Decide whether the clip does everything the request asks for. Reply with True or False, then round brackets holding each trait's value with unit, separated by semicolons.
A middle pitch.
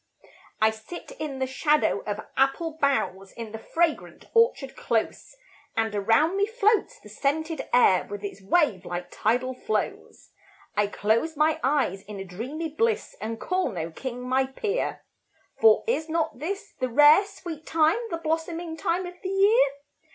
False (300 Hz)